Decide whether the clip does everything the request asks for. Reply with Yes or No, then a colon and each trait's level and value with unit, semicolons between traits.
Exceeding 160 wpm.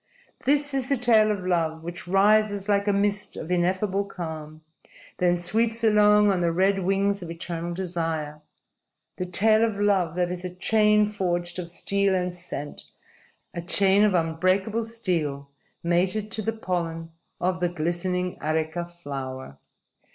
No: average, 155 wpm